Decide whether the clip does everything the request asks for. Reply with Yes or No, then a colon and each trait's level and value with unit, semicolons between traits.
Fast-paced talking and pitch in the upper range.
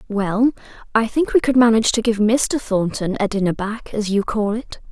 Yes: fast, 210 wpm; high, 220 Hz